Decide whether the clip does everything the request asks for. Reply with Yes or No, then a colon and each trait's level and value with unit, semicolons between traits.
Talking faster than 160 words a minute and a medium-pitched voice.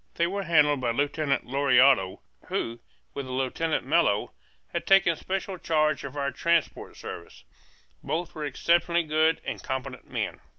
No: average, 140 wpm; medium, 150 Hz